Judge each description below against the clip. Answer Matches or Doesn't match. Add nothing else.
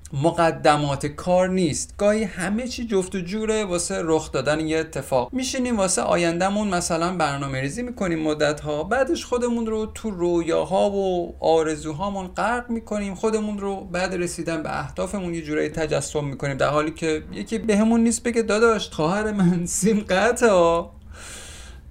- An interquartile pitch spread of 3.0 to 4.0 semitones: Doesn't match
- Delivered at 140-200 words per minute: Matches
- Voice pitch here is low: Doesn't match